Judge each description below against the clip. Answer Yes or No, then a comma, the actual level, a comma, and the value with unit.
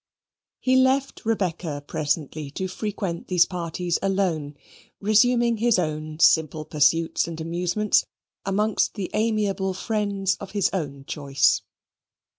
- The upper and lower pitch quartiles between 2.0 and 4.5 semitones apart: No, average, 5.0 semitones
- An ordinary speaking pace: No, slow, 115 wpm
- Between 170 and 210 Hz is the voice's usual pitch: Yes, medium, 185 Hz